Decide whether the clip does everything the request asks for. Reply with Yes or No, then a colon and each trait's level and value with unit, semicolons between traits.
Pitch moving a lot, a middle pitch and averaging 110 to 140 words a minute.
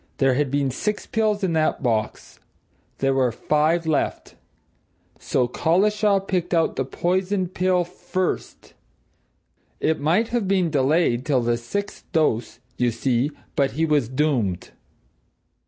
Yes: wide, 6.0 semitones; medium, 155 Hz; slow, 135 wpm